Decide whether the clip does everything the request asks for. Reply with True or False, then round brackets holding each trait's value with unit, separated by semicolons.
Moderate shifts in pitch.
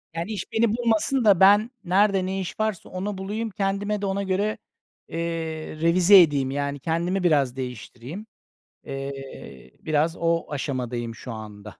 False (6.8 semitones)